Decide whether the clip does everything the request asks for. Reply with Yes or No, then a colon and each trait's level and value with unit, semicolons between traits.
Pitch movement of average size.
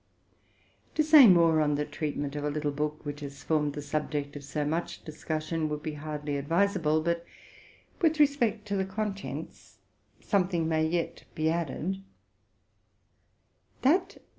Yes: average, 4.2 semitones